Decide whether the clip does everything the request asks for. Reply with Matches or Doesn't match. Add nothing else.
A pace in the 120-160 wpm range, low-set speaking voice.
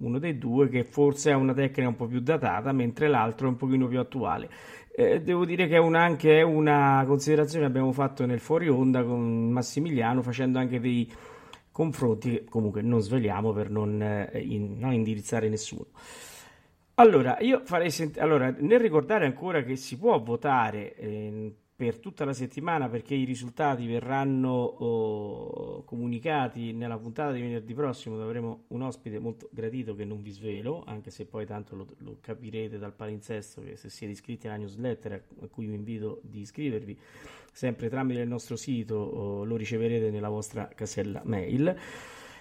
Doesn't match